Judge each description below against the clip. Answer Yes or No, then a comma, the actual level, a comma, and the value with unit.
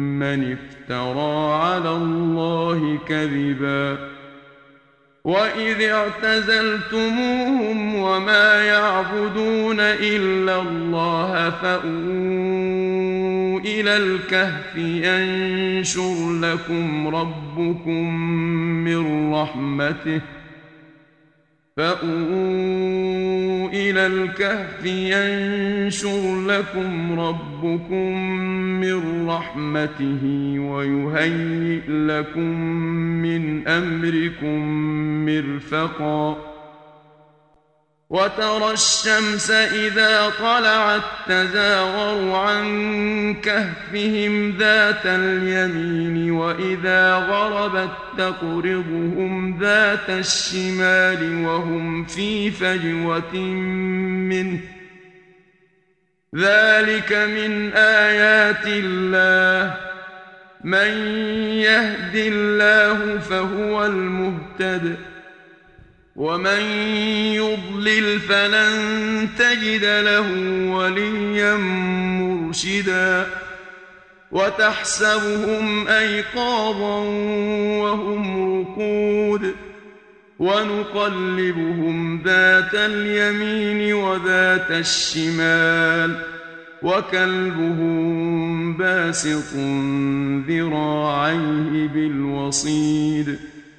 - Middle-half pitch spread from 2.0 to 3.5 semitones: No, average, 4.0 semitones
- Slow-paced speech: Yes, slow, 50 wpm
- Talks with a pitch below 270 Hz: Yes, medium, 185 Hz